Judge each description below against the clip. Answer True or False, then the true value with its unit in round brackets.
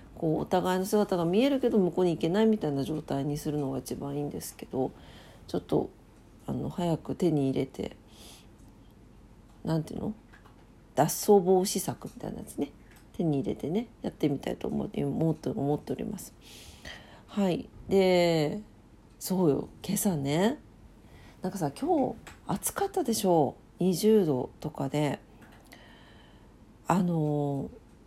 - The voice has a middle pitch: True (160 Hz)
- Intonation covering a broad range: True (6.0 semitones)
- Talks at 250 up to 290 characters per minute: True (270 characters per minute)